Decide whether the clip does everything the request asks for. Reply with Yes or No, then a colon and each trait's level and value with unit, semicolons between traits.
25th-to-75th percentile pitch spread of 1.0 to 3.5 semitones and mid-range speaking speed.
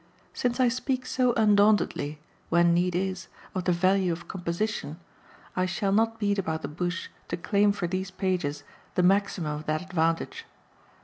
Yes: average, 3.1 semitones; average, 165 wpm